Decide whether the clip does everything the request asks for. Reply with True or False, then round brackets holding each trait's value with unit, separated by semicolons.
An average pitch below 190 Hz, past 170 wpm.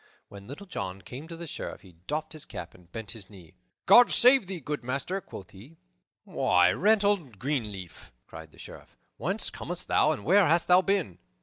True (140 Hz; 190 wpm)